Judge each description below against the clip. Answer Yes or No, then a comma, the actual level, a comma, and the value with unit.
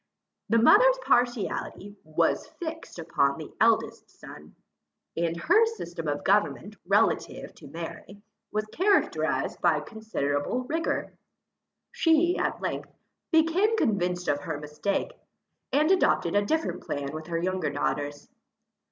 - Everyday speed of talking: No, slow, 125 wpm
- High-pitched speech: Yes, high, 205 Hz